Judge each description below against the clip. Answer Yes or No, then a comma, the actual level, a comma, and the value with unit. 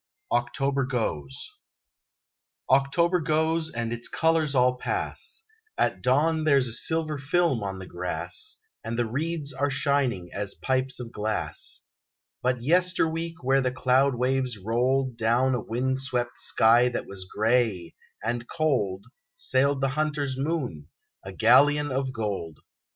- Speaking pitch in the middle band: No, low, 130 Hz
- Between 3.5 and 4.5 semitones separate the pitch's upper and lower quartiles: Yes, average, 3.9 semitones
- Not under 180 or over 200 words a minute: No, slow, 135 wpm